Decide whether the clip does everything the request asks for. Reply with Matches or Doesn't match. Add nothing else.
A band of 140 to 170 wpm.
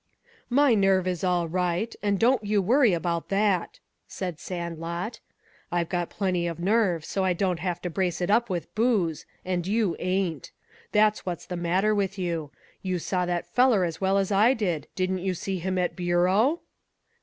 Doesn't match